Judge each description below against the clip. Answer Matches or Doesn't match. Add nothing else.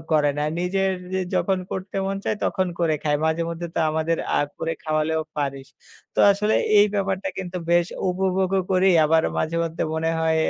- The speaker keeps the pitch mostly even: Doesn't match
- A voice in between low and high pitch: Matches